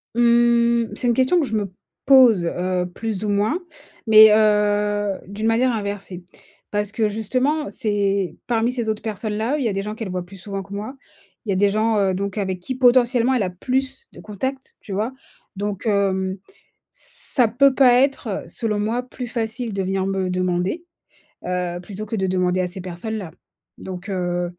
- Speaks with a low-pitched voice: No, high, 210 Hz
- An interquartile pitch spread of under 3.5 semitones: No, average, 3.8 semitones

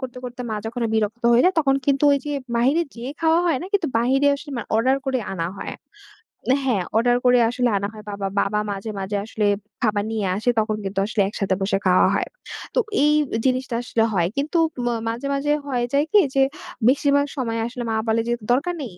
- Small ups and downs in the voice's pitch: No, average, 4.3 semitones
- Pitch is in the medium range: No, high, 245 Hz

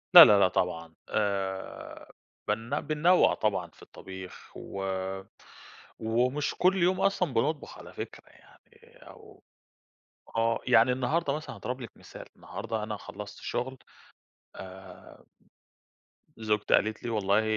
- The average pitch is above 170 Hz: No, low, 115 Hz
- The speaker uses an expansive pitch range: Yes, wide, 5.9 semitones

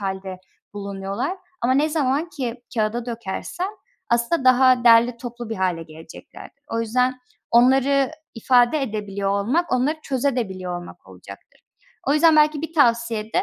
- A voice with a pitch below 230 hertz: No, high, 240 Hz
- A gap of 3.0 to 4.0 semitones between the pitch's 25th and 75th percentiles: No, average, 4.7 semitones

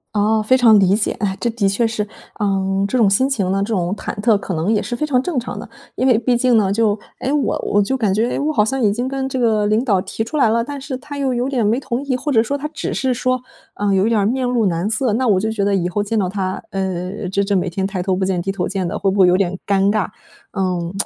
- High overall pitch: Yes, high, 215 Hz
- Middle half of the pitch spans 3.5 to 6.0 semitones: Yes, average, 4.3 semitones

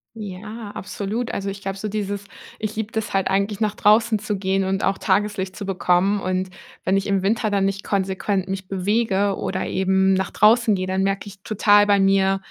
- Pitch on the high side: Yes, high, 195 Hz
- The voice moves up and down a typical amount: No, narrow, 1.5 semitones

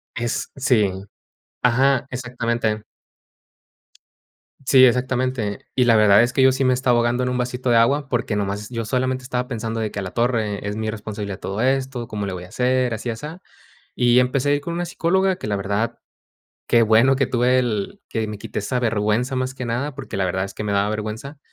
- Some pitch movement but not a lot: Yes, average, 3.1 semitones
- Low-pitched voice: Yes, low, 120 Hz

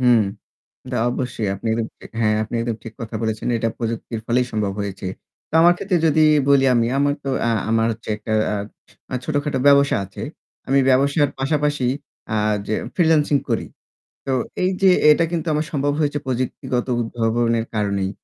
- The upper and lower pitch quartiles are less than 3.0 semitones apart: No, average, 4.3 semitones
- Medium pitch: No, low, 125 Hz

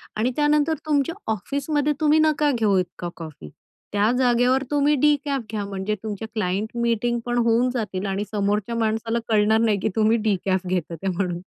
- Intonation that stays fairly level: No, average, 4.9 semitones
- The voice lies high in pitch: Yes, high, 220 Hz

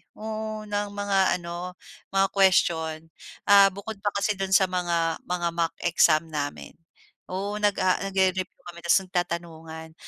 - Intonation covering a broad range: No, average, 2.7 semitones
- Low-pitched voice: No, medium, 185 Hz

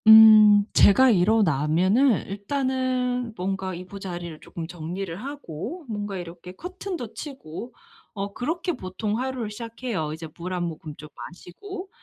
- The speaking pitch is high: Yes, high, 205 Hz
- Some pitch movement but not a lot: No, wide, 6.2 semitones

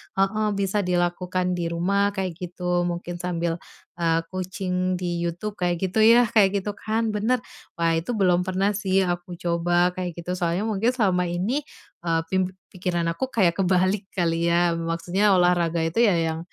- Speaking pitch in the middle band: Yes, medium, 180 Hz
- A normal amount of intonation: No, narrow, 2.2 semitones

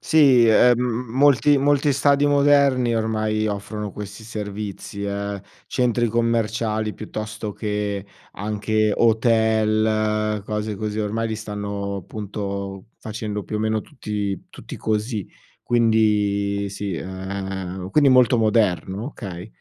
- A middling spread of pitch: No, narrow, 2.1 semitones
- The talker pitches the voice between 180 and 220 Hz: No, low, 110 Hz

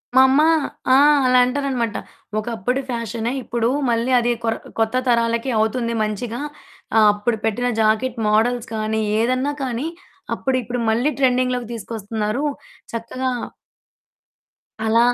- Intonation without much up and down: Yes, narrow, 2.2 semitones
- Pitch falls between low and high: No, high, 235 Hz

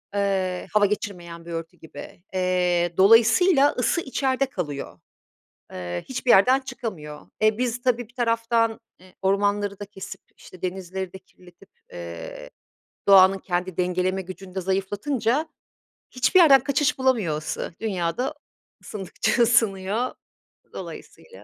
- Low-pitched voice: No, high, 195 Hz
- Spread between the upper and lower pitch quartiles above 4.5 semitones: Yes, average, 5.0 semitones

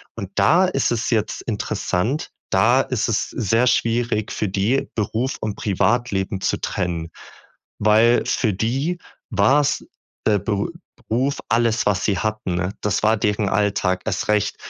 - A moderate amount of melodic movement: Yes, average, 3.3 semitones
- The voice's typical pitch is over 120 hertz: No, low, 110 Hz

